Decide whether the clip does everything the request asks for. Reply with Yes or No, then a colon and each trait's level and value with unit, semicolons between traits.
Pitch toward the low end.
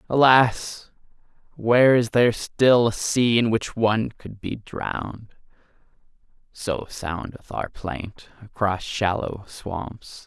Yes: low, 110 Hz